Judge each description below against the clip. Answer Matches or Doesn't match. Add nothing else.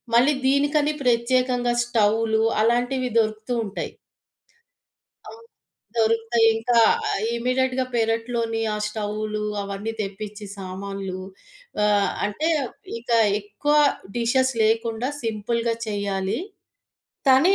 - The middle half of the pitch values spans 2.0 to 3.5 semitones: Matches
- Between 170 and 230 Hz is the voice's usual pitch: Matches